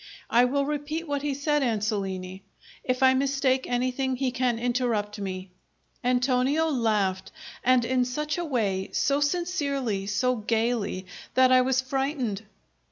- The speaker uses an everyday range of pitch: Yes, average, 4.0 semitones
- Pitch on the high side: Yes, very high, 255 Hz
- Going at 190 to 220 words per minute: No, average, 140 wpm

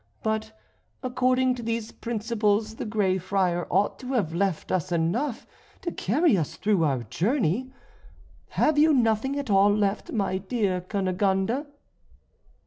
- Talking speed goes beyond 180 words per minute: No, slow, 135 wpm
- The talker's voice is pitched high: Yes, high, 210 Hz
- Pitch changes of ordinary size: Yes, average, 4.7 semitones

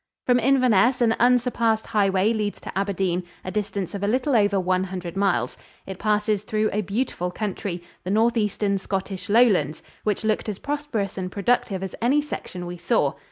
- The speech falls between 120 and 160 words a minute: No, average, 170 wpm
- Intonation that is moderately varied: Yes, average, 3.2 semitones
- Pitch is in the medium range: No, high, 205 Hz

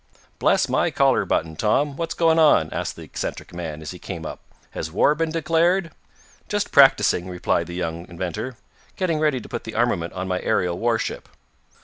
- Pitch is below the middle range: Yes, low, 110 Hz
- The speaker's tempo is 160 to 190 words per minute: Yes, average, 185 wpm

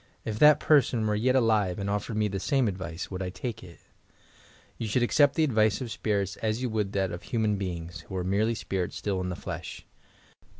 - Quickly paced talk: Yes, fast, 215 wpm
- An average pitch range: Yes, average, 3.5 semitones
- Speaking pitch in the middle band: No, low, 105 Hz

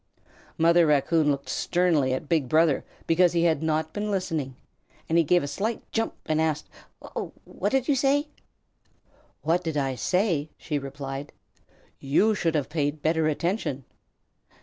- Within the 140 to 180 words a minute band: Yes, average, 155 wpm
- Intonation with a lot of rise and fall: No, average, 3.6 semitones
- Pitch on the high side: No, medium, 160 Hz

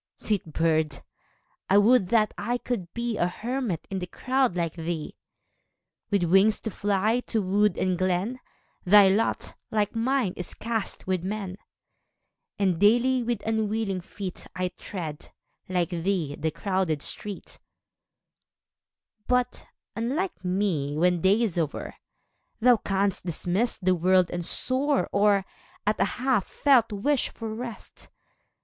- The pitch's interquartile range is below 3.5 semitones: No, average, 4.2 semitones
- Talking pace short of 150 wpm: Yes, average, 140 wpm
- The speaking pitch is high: Yes, high, 200 Hz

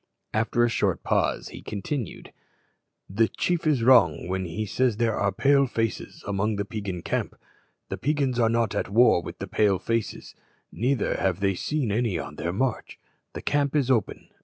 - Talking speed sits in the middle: Yes, average, 180 wpm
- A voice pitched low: Yes, low, 115 Hz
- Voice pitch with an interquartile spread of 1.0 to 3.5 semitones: No, average, 4.6 semitones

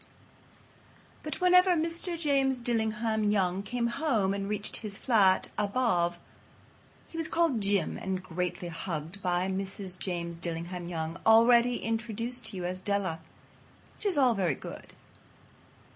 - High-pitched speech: Yes, high, 205 Hz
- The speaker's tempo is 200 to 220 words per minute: No, slow, 135 wpm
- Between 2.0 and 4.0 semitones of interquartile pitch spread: No, average, 5.1 semitones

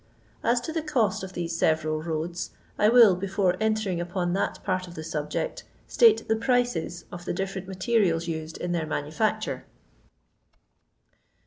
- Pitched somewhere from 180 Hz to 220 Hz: Yes, medium, 185 Hz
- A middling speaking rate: Yes, average, 150 wpm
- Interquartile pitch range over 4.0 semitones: Yes, average, 4.7 semitones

